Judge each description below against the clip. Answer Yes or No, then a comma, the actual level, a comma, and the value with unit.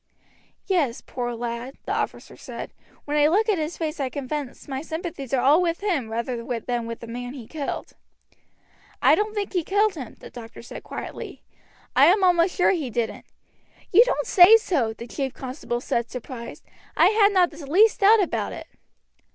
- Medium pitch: No, very high, 295 Hz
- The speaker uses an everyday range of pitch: No, wide, 7.2 semitones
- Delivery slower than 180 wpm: No, average, 185 wpm